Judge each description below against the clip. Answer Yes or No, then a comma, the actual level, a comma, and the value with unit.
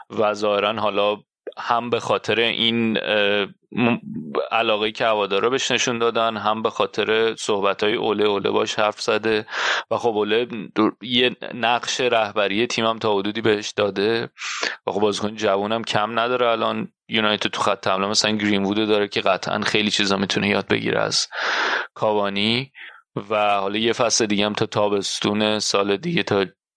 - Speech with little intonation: Yes, narrow, 1.6 semitones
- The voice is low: Yes, low, 105 Hz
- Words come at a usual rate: No, fast, 160 wpm